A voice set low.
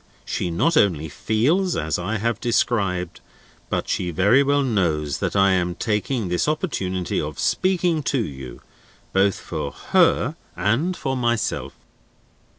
Yes: low, 105 Hz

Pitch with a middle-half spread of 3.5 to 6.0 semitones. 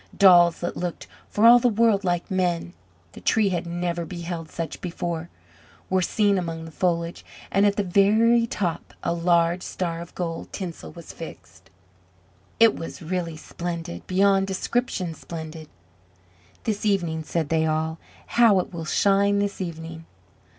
No: average, 3.1 semitones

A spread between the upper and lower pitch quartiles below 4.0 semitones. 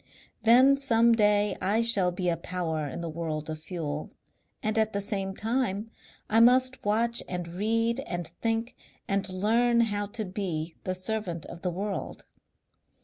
No: average, 4.4 semitones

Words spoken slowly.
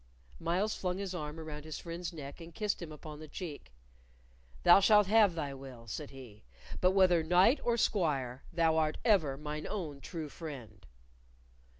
No: average, 170 wpm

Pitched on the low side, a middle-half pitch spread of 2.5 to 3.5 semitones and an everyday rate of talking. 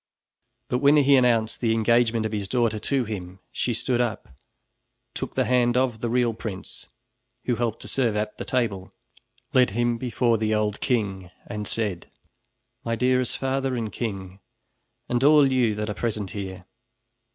Yes: low, 115 Hz; average, 2.9 semitones; average, 165 wpm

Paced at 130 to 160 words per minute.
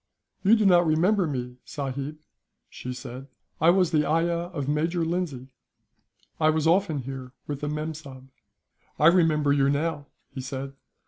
Yes: average, 155 wpm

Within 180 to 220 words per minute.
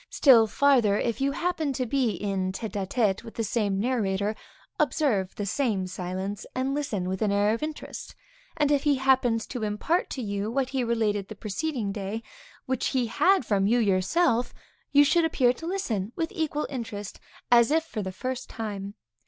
Yes: average, 185 wpm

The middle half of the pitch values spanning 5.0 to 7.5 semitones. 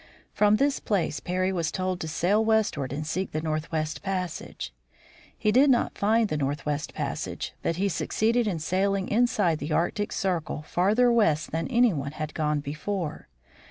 Yes: average, 5.3 semitones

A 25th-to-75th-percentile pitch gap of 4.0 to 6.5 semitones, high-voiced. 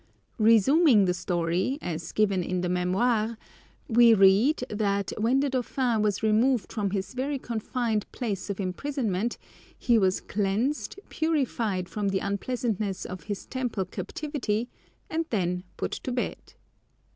Yes: average, 4.5 semitones; high, 215 Hz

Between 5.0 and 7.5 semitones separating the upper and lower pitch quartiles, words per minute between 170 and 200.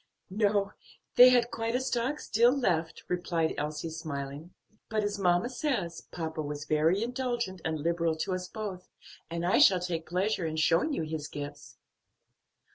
No: wide, 5.4 semitones; average, 160 wpm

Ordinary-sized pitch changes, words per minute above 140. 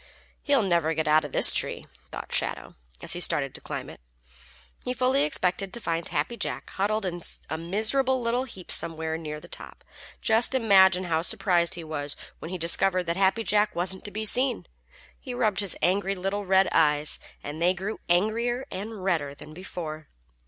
Yes: average, 4.7 semitones; average, 185 wpm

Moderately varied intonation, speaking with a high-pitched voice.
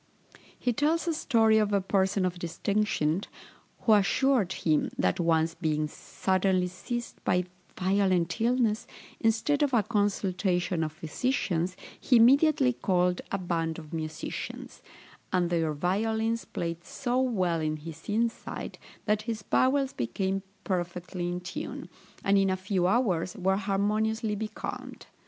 Yes: average, 4.2 semitones; high, 195 Hz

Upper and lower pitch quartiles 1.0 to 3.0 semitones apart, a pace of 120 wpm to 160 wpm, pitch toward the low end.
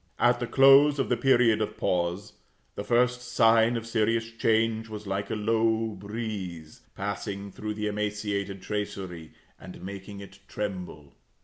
Yes: narrow, 2.5 semitones; average, 145 wpm; low, 105 Hz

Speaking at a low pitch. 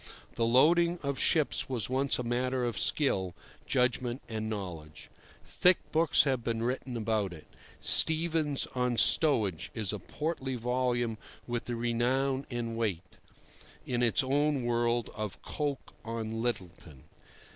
Yes: low, 120 Hz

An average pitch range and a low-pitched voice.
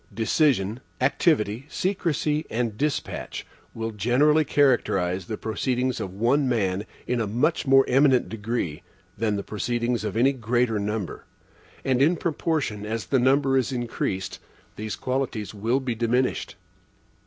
Yes: average, 3.9 semitones; low, 120 Hz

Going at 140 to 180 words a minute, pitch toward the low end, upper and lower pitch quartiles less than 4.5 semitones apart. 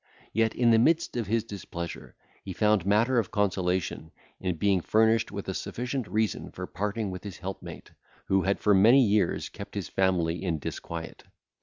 Yes: average, 175 wpm; low, 100 Hz; average, 3.2 semitones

